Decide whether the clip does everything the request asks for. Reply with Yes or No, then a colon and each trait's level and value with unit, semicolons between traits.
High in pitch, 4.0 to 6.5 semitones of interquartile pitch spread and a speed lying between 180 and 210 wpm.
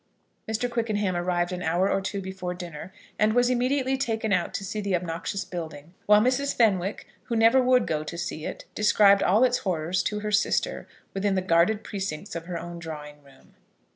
Yes: high, 195 Hz; average, 4.3 semitones; average, 195 wpm